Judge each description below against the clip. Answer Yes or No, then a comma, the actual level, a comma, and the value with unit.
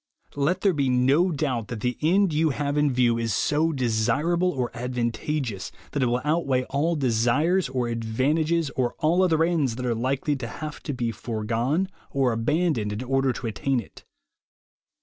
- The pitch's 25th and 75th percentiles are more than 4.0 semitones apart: Yes, average, 4.5 semitones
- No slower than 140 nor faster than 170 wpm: No, average, 180 wpm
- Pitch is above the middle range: No, low, 135 Hz